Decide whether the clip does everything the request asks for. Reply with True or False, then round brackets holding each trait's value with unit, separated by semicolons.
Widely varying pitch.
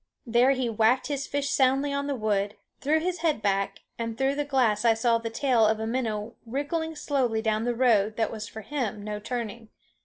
False (4.0 semitones)